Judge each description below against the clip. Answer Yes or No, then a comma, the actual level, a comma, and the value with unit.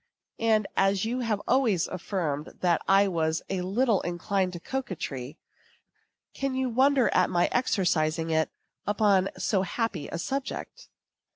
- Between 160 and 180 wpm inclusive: No, slow, 135 wpm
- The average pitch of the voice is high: Yes, high, 195 Hz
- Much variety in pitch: No, average, 5.0 semitones